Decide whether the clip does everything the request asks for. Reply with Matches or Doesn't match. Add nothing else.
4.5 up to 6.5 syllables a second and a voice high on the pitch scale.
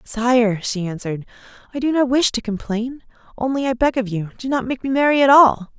Matches